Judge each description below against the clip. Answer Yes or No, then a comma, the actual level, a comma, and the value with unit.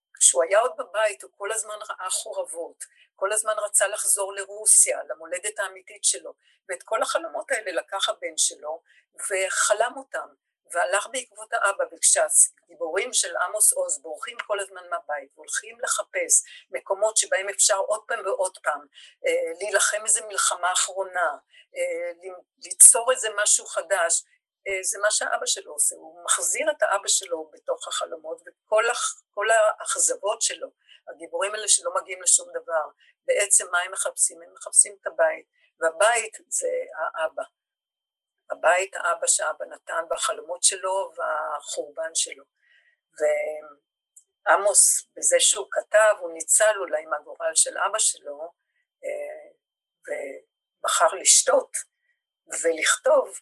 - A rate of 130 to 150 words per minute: No, average, 120 wpm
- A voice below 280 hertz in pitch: No, very high, 285 Hz